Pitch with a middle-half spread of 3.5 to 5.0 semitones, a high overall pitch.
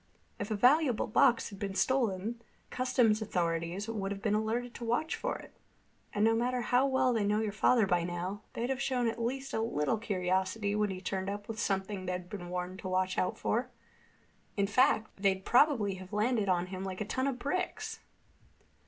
Yes: average, 4.3 semitones; high, 210 Hz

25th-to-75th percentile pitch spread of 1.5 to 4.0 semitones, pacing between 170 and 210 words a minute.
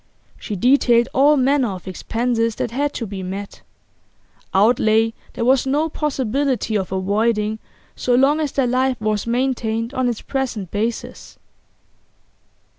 No: average, 3.6 semitones; slow, 135 wpm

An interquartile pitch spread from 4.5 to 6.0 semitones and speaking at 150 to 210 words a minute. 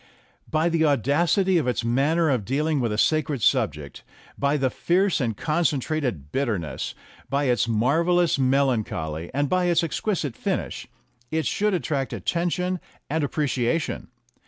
No: average, 5.2 semitones; average, 140 wpm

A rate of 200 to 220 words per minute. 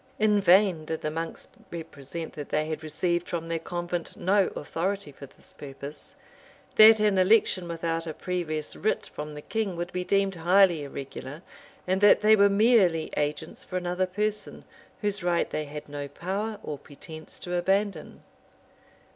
No: average, 165 wpm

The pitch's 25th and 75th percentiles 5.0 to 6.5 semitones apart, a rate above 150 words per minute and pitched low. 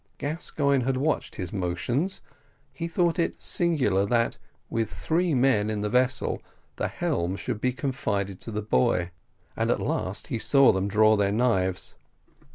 Yes: wide, 5.6 semitones; average, 160 wpm; low, 115 Hz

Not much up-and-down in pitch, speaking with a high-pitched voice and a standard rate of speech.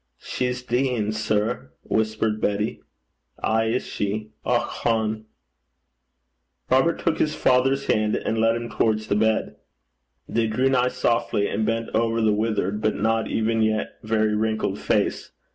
No: narrow, 1.5 semitones; low, 110 Hz; average, 145 wpm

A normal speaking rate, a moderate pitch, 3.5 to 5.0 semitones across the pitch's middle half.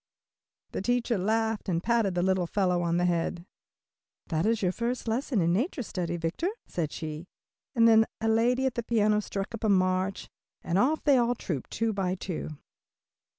No: average, 185 wpm; high, 200 Hz; average, 4.6 semitones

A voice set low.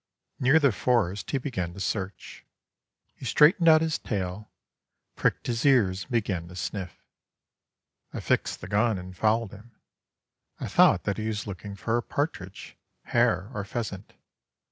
Yes: low, 105 Hz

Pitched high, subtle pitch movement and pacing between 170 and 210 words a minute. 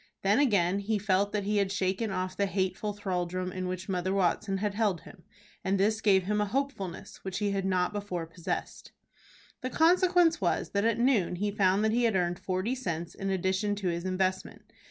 Yes: high, 195 Hz; narrow, 2.3 semitones; average, 200 wpm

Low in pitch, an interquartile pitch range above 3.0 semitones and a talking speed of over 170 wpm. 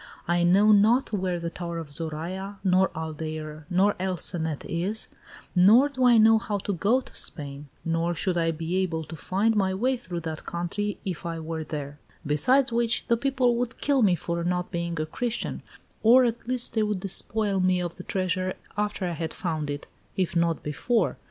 No: medium, 185 Hz; average, 4.5 semitones; average, 195 wpm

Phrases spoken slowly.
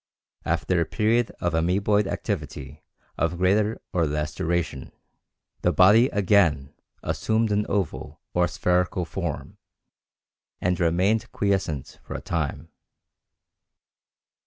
Yes: slow, 110 wpm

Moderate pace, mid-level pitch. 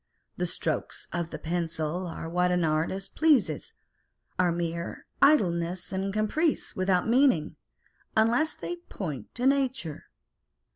No: slow, 125 wpm; medium, 180 Hz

